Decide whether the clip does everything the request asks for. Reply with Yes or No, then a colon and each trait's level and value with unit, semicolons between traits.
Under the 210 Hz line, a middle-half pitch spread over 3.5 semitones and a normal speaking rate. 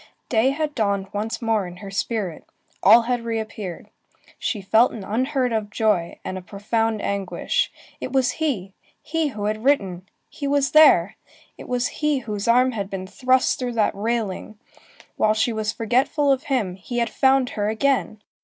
No: high, 225 Hz; average, 4.1 semitones; average, 175 wpm